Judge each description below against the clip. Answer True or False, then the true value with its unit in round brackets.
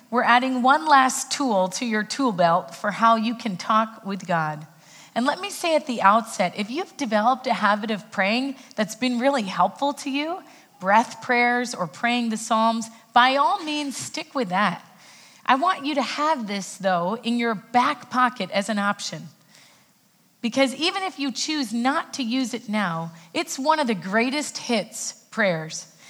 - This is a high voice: True (235 Hz)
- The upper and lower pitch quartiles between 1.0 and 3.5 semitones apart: False (5.1 semitones)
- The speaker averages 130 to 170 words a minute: False (180 wpm)